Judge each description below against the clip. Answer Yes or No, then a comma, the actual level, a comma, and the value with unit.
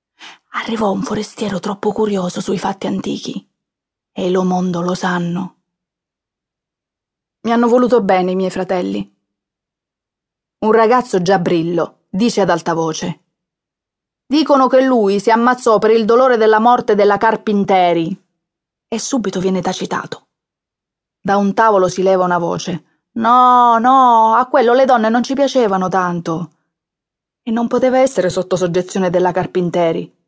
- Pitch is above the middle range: Yes, high, 195 Hz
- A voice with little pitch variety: No, average, 4.2 semitones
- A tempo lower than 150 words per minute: Yes, average, 135 wpm